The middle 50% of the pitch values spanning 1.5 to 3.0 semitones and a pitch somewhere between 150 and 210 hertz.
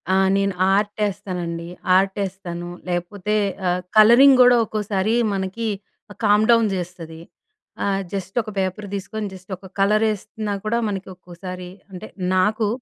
Yes: narrow, 2.6 semitones; high, 195 Hz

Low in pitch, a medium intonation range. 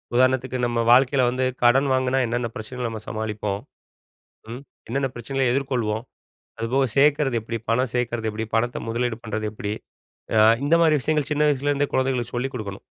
Yes: low, 125 Hz; average, 3.0 semitones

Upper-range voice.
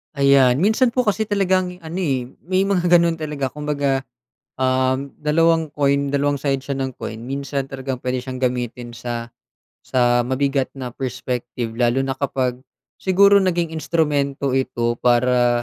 No: medium, 140 Hz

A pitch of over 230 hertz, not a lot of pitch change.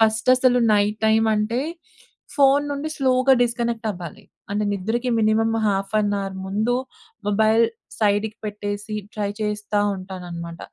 No: high, 215 Hz; narrow, 2.3 semitones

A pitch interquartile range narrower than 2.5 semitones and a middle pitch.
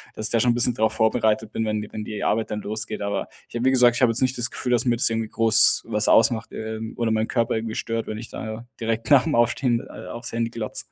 No: narrow, 1.4 semitones; low, 115 Hz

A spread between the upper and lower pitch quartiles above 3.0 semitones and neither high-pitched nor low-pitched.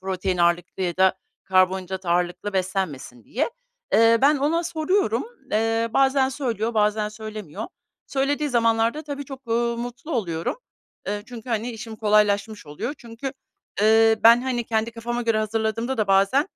No: average, 3.8 semitones; high, 225 Hz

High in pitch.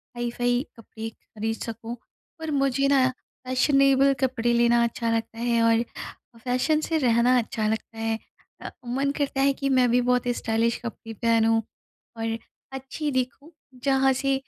Yes: high, 245 Hz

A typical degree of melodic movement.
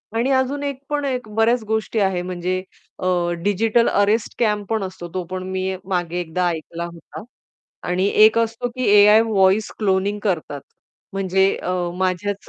Yes: average, 3.5 semitones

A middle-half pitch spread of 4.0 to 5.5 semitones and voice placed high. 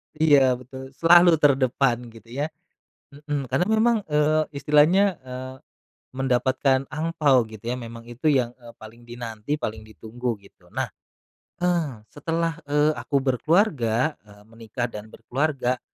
No: average, 4.3 semitones; low, 130 Hz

